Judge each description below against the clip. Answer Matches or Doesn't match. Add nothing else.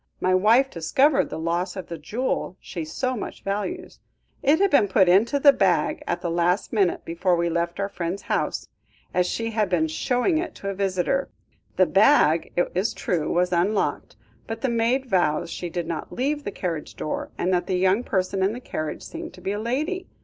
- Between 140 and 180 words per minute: Doesn't match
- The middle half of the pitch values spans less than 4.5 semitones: Doesn't match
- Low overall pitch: Doesn't match